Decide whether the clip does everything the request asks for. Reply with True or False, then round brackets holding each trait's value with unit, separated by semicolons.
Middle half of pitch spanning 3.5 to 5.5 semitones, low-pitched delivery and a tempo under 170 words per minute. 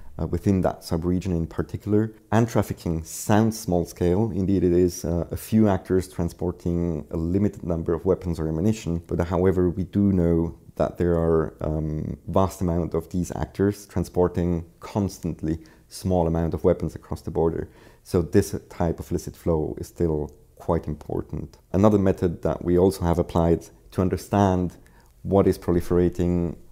False (2.4 semitones; 90 Hz; 160 wpm)